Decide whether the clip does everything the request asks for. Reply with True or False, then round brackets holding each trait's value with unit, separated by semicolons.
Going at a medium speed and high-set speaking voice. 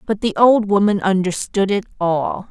True (165 wpm; 200 Hz)